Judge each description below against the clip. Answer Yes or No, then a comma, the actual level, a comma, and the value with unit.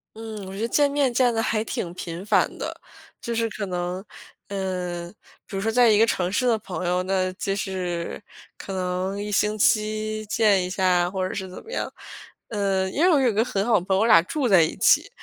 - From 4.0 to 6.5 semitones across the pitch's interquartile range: No, average, 3.3 semitones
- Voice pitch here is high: Yes, high, 200 Hz